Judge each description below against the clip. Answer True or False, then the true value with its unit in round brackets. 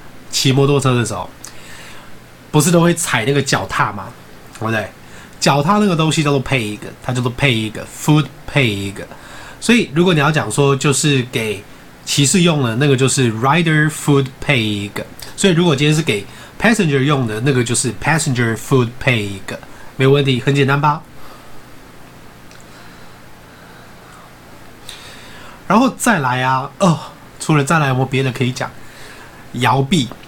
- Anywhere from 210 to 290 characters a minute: True (275 characters per minute)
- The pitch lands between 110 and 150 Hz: True (135 Hz)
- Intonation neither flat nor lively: True (4.5 semitones)